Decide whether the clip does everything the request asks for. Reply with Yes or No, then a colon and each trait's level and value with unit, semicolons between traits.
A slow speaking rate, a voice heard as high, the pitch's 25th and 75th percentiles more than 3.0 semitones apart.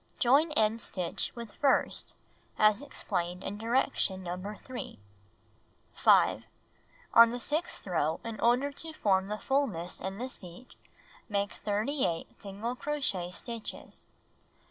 Yes: slow, 120 wpm; high, 215 Hz; average, 5.1 semitones